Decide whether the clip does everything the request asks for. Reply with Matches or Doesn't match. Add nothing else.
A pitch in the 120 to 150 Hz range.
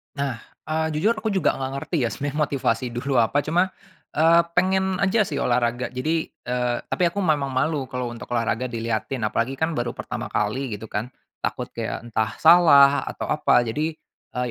Matches